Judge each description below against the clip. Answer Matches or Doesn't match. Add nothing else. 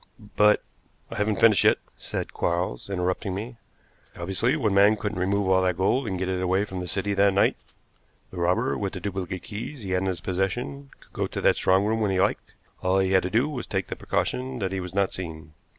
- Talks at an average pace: Doesn't match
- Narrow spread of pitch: Matches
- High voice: Doesn't match